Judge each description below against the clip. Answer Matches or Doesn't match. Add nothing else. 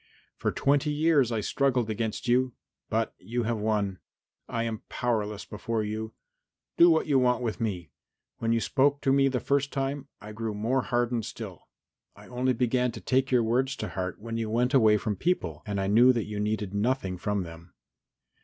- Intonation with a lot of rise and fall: Doesn't match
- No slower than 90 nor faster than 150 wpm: Doesn't match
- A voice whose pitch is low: Matches